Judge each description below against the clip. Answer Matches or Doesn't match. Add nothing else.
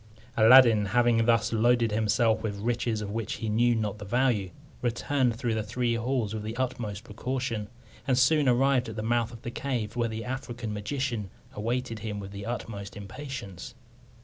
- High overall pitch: Doesn't match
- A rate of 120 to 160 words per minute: Doesn't match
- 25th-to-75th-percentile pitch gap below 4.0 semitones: Matches